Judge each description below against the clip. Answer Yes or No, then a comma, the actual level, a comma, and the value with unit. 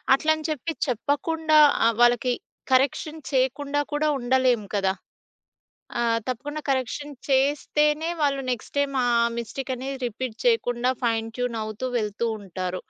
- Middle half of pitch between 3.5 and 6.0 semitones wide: Yes, average, 3.8 semitones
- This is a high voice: Yes, very high, 260 Hz